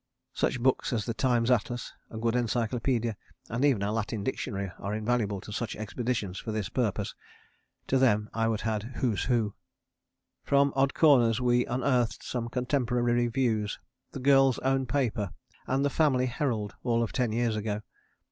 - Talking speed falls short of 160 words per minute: No, average, 165 wpm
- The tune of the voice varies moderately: Yes, average, 3.0 semitones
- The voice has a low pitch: Yes, low, 120 Hz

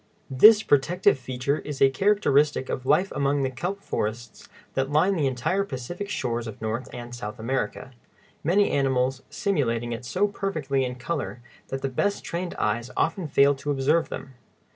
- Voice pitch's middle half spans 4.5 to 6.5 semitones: Yes, average, 5.2 semitones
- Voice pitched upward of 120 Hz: Yes, low, 135 Hz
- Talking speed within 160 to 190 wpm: Yes, average, 170 wpm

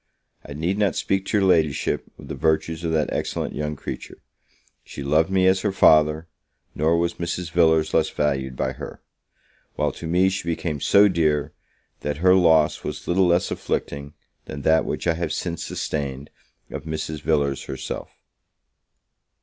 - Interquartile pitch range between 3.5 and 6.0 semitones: No, average, 2.7 semitones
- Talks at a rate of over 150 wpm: Yes, average, 165 wpm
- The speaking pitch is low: Yes, very low, 80 Hz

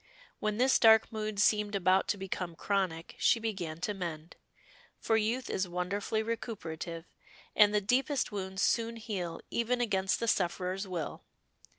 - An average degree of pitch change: Yes, average, 3.5 semitones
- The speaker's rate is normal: Yes, average, 150 wpm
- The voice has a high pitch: Yes, high, 200 Hz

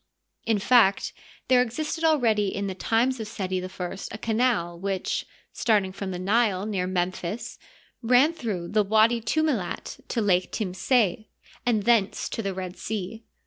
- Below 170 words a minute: Yes, average, 150 wpm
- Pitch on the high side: Yes, high, 210 Hz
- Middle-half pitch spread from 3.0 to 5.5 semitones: Yes, average, 3.9 semitones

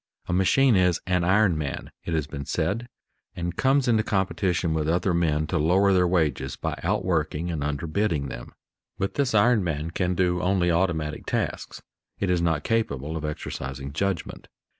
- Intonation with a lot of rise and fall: No, average, 3.8 semitones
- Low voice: Yes, very low, 85 Hz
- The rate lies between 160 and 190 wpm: Yes, average, 170 wpm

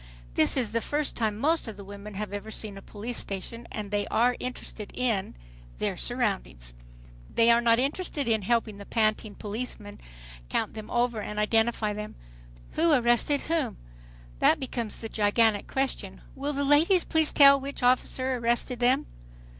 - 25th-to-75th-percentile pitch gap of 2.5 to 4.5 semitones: Yes, average, 3.7 semitones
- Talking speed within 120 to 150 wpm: No, average, 165 wpm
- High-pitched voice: Yes, high, 230 Hz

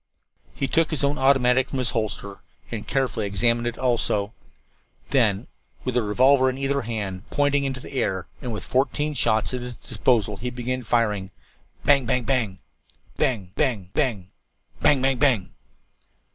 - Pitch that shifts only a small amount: No, average, 3.8 semitones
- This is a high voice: No, low, 125 Hz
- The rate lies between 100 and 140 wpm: No, average, 160 wpm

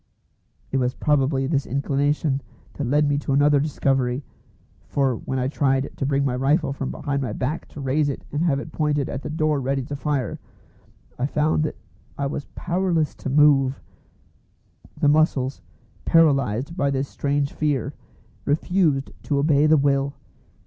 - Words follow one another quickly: No, average, 165 wpm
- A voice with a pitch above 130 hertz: Yes, medium, 140 Hz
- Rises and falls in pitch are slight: Yes, narrow, 1.7 semitones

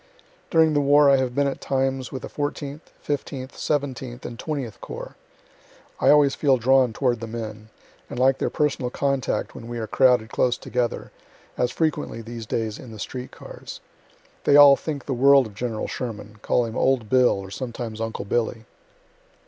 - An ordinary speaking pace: Yes, average, 180 wpm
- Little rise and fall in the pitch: No, average, 3.3 semitones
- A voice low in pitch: Yes, low, 125 Hz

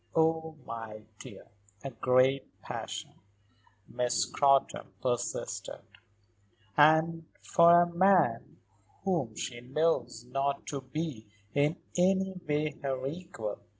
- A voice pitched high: No, medium, 145 Hz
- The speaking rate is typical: No, slow, 105 wpm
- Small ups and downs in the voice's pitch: No, average, 4.9 semitones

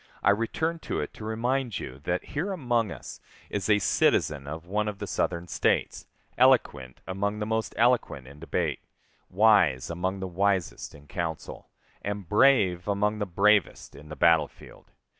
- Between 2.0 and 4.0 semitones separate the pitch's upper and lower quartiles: No, average, 4.5 semitones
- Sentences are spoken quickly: No, average, 165 wpm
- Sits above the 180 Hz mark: No, low, 100 Hz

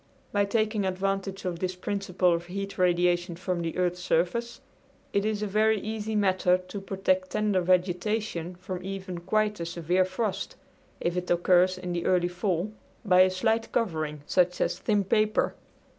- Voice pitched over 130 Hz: Yes, medium, 185 Hz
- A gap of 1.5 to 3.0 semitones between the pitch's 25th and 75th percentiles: Yes, average, 2.7 semitones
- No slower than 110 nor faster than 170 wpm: Yes, average, 165 wpm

